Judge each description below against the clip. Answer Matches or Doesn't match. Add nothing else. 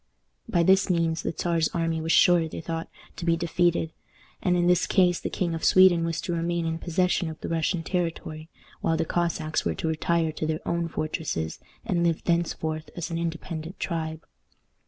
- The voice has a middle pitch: Matches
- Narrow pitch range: Matches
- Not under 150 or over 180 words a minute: Doesn't match